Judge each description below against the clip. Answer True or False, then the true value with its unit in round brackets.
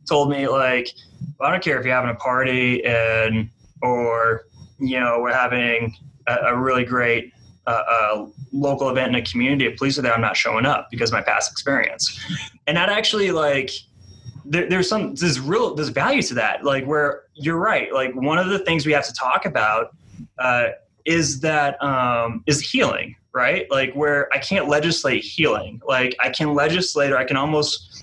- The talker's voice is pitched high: False (135 Hz)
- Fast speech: False (190 wpm)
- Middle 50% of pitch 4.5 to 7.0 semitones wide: False (3.5 semitones)